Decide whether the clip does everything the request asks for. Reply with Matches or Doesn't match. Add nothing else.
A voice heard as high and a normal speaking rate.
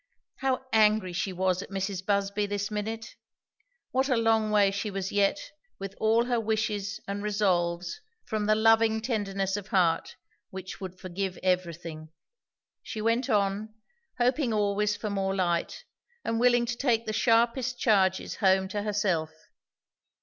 Matches